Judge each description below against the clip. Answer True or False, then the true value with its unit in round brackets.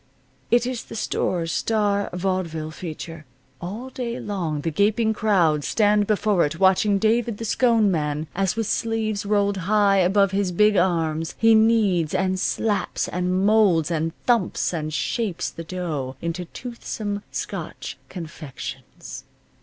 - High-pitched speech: True (195 Hz)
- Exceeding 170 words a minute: False (140 wpm)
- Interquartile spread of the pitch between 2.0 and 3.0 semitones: False (4.3 semitones)